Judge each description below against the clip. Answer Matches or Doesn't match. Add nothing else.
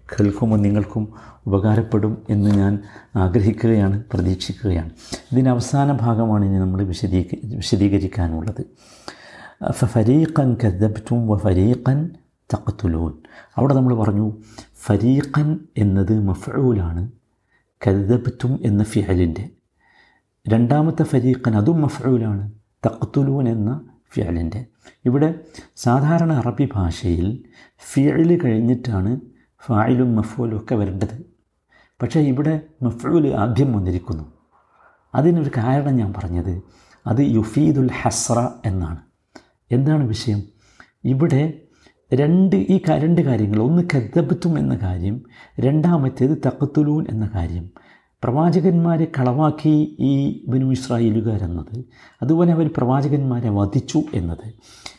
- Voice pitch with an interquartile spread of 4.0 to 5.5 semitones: Matches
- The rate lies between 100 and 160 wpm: Doesn't match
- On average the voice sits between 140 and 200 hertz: Doesn't match